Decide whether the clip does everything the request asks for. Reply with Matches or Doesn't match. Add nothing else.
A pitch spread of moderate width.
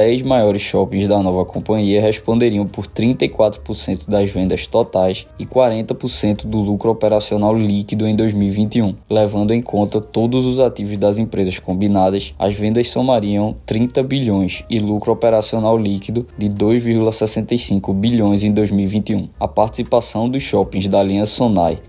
Doesn't match